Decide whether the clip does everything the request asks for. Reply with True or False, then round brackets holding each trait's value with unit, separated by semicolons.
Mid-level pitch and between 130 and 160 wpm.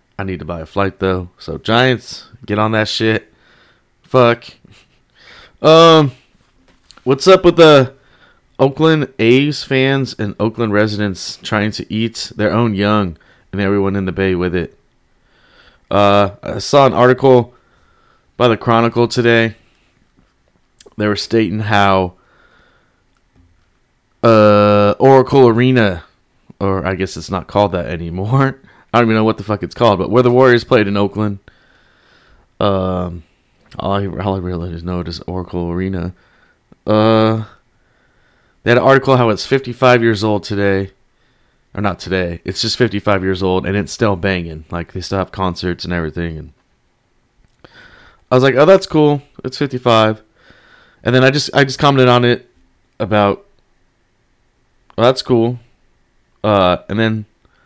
False (105 Hz; 150 wpm)